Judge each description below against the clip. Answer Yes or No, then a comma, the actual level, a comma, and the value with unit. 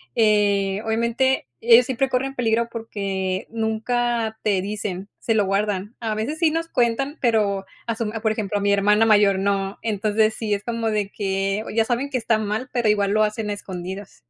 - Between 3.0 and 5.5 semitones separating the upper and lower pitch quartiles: No, narrow, 2.4 semitones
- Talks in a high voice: Yes, high, 215 Hz